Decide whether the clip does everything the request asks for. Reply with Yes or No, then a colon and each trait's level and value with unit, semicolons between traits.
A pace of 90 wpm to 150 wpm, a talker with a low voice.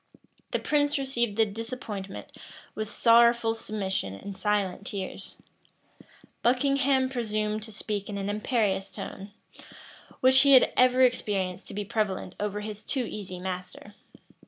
No: slow, 135 wpm; high, 215 Hz